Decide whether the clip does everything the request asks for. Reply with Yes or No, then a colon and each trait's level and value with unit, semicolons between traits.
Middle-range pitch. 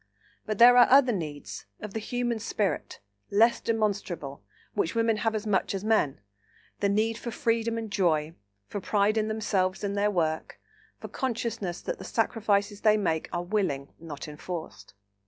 No: high, 205 Hz